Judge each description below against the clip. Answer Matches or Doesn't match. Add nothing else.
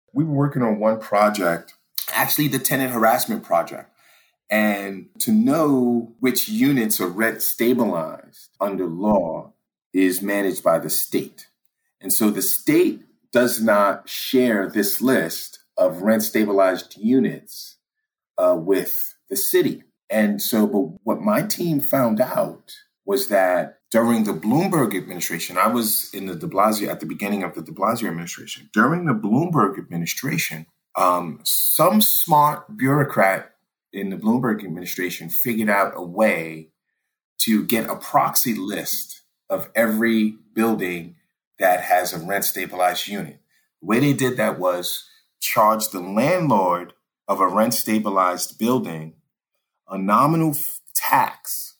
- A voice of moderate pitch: Doesn't match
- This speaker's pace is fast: Doesn't match